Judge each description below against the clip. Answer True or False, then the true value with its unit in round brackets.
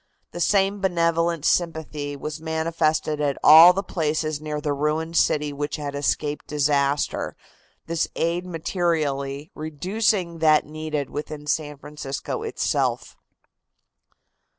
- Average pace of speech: False (115 wpm)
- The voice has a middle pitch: True (155 Hz)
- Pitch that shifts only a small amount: True (2.2 semitones)